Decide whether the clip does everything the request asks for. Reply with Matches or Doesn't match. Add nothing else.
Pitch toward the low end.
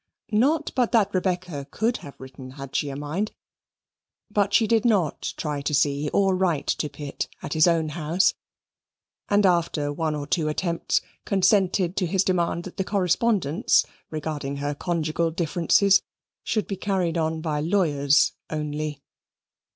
Doesn't match